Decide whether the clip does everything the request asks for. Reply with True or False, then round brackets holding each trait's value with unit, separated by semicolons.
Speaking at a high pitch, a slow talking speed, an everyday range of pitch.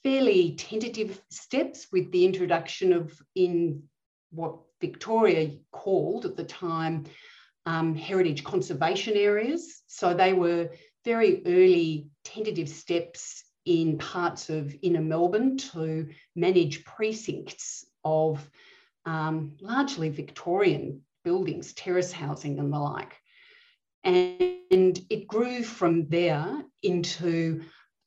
False (175 Hz; 105 wpm; 5.0 semitones)